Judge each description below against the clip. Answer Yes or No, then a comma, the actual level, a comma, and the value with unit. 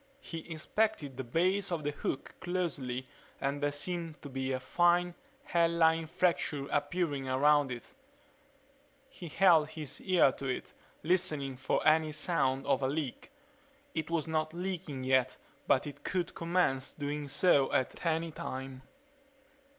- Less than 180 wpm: Yes, average, 145 wpm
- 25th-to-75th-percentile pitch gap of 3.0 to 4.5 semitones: Yes, average, 4.0 semitones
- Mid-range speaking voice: Yes, medium, 155 Hz